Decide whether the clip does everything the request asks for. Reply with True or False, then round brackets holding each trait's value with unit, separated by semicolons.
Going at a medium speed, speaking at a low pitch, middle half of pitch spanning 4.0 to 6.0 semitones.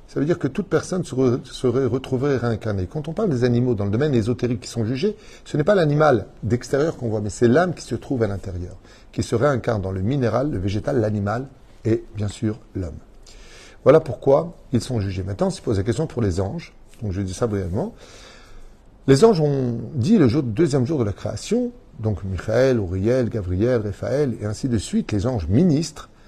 True (205 wpm; 120 Hz; 4.7 semitones)